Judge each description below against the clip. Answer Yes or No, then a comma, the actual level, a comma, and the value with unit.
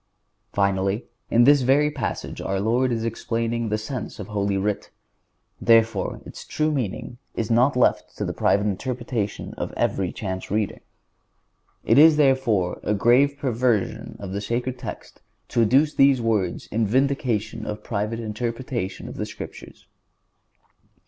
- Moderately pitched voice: No, low, 115 Hz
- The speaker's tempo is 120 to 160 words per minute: Yes, average, 145 wpm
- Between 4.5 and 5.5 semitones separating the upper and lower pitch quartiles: No, average, 3.7 semitones